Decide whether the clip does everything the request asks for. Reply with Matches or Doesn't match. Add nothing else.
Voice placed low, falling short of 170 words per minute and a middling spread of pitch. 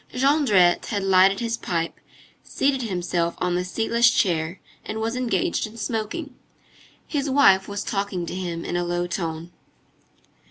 Doesn't match